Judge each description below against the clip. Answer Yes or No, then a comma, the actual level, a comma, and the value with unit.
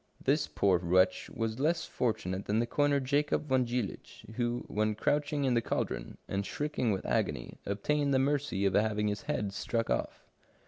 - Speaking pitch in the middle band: No, low, 115 Hz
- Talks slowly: No, average, 175 wpm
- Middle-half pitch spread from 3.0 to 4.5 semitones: No, wide, 5.5 semitones